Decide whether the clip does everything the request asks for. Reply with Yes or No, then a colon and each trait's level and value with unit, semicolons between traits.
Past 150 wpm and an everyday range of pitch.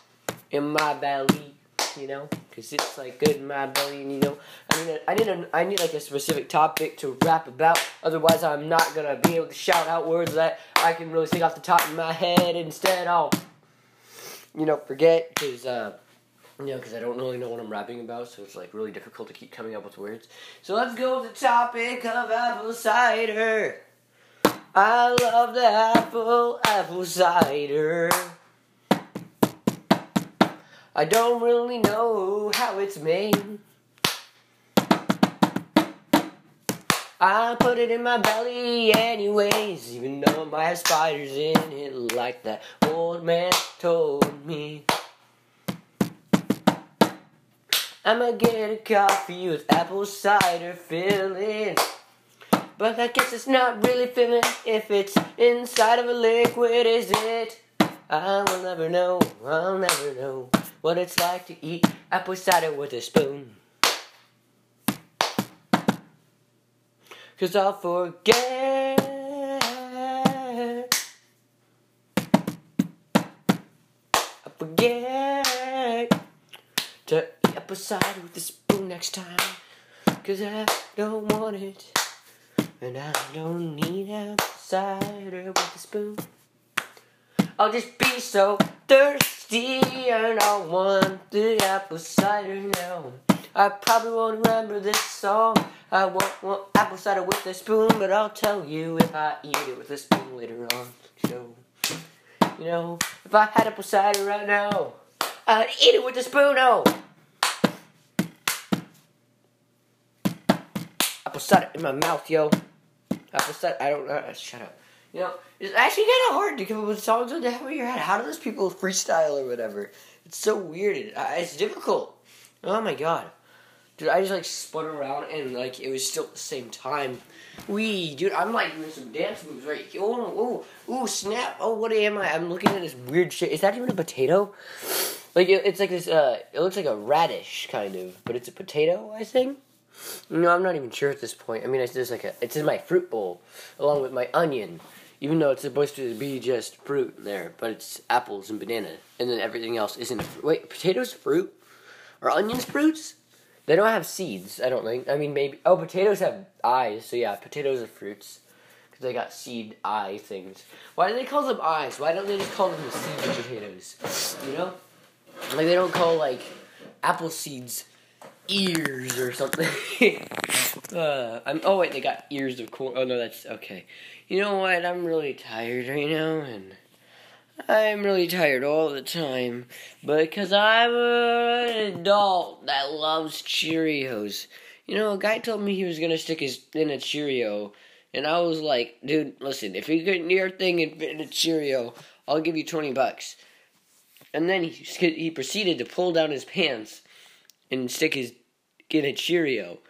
No: average, 165 wpm; wide, 6.5 semitones